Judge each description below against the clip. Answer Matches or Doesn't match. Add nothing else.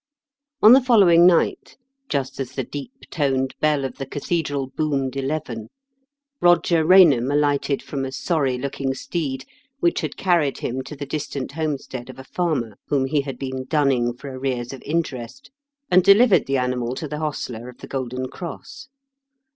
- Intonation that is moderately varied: Matches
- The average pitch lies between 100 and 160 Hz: Matches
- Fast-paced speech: Doesn't match